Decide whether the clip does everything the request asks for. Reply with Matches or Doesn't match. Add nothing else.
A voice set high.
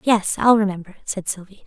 Matches